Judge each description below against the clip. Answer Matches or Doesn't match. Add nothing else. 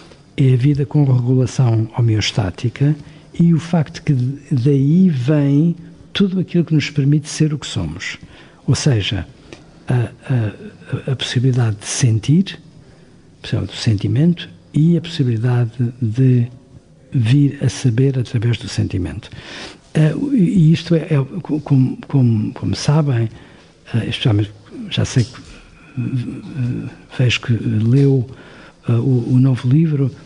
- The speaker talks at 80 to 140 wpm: Matches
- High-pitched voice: Doesn't match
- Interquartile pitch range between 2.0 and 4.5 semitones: Matches